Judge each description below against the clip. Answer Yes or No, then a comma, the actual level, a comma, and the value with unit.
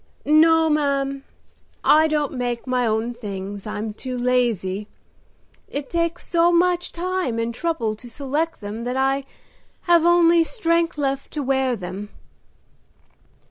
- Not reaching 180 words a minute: Yes, slow, 135 wpm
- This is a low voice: No, very high, 275 Hz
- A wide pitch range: Yes, wide, 5.9 semitones